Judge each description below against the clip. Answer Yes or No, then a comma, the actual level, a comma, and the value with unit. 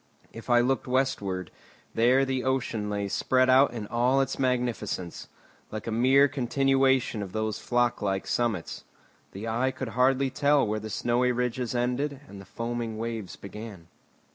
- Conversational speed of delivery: Yes, average, 160 wpm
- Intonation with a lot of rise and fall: No, average, 3.2 semitones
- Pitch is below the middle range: Yes, low, 120 Hz